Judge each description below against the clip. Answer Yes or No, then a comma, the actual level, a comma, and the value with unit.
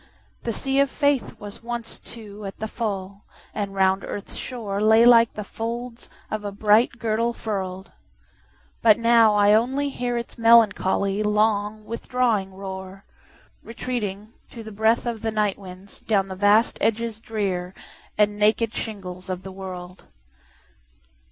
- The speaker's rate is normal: No, slow, 125 wpm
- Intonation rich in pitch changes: No, average, 2.7 semitones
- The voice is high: Yes, high, 215 Hz